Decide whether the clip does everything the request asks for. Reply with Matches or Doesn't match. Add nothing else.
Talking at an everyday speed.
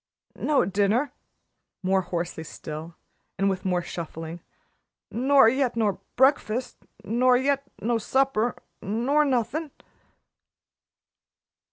Doesn't match